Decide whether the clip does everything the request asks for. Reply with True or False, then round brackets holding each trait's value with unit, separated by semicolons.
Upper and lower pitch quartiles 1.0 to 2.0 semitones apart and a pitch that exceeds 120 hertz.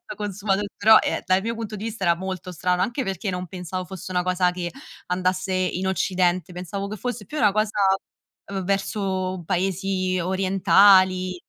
True (1.6 semitones; 185 Hz)